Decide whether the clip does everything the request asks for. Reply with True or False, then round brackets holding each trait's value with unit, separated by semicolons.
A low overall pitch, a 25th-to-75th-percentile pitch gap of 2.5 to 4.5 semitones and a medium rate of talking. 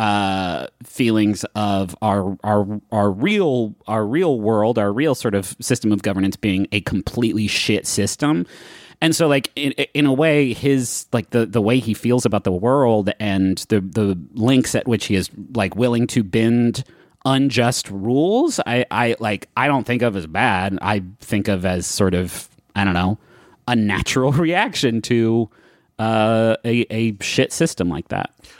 True (110 Hz; 3.5 semitones; 170 wpm)